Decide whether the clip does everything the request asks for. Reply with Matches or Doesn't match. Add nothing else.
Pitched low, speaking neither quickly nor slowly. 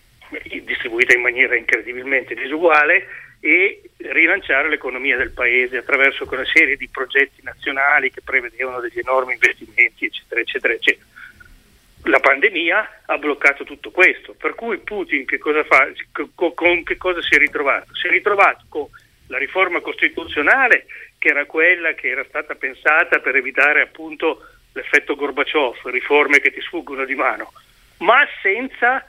Doesn't match